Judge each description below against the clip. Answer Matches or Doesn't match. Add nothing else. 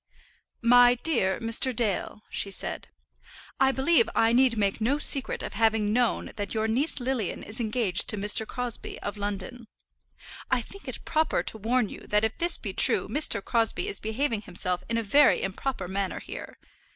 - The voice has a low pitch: Doesn't match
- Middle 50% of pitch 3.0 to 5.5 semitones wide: Matches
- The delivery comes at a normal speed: Matches